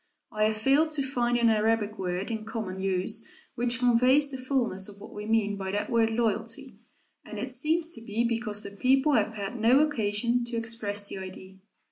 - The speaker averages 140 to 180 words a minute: No, average, 195 wpm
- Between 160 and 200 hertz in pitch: No, high, 225 Hz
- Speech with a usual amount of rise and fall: Yes, average, 3.3 semitones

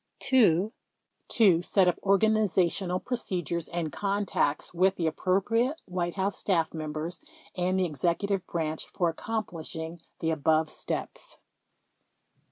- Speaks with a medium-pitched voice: Yes, medium, 180 Hz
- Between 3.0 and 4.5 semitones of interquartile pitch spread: Yes, average, 3.4 semitones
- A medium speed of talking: No, slow, 120 wpm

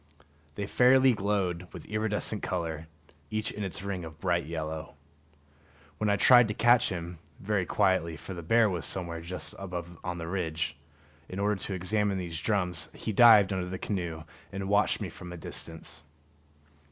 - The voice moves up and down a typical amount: Yes, average, 3.4 semitones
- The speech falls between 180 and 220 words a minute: No, average, 170 wpm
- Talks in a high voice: No, very low, 95 Hz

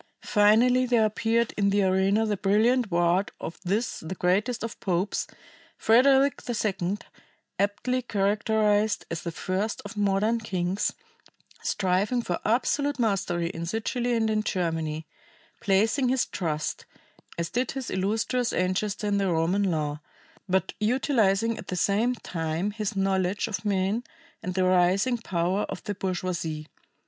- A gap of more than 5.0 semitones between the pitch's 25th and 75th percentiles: No, average, 3.6 semitones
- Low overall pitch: No, high, 200 Hz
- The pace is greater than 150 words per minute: No, average, 140 wpm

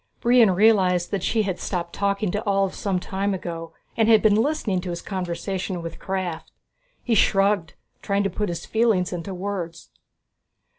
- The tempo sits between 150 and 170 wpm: Yes, average, 165 wpm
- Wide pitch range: No, average, 2.7 semitones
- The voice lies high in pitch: Yes, high, 195 Hz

